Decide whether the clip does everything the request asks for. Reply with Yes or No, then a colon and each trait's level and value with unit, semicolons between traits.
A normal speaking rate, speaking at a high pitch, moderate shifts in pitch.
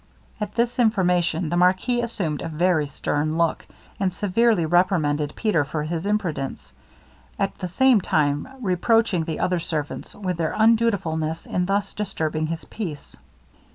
No: average, 145 wpm; medium, 180 Hz; average, 4.6 semitones